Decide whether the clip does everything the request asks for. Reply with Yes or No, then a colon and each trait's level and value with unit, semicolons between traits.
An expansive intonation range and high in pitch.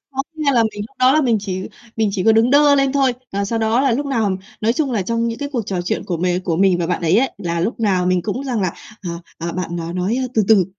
Yes: wide, 5.7 semitones; high, 220 Hz